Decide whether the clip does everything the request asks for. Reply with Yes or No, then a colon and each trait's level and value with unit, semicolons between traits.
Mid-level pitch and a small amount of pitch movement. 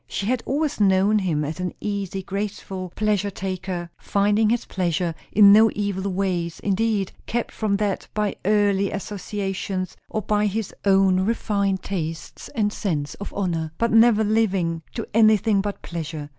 No: high, 200 Hz; narrow, 2.3 semitones